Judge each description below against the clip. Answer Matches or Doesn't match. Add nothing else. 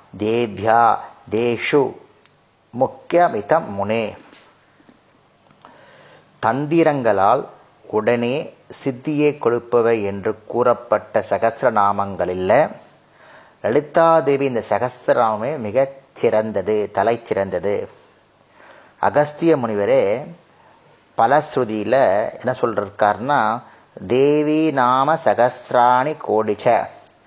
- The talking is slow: Matches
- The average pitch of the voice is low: Matches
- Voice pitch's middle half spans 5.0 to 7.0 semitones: Matches